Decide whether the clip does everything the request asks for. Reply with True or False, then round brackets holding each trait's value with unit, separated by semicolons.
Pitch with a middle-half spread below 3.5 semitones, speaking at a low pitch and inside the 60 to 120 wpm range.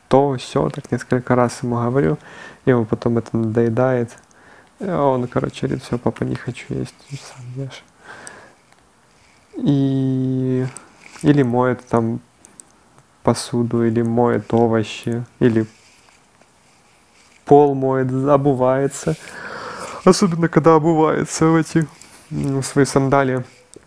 True (2.9 semitones; 130 Hz; 105 wpm)